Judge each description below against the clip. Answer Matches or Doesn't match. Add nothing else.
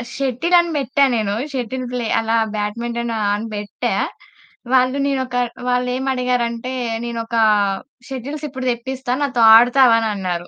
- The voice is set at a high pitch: Matches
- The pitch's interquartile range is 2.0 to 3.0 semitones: Matches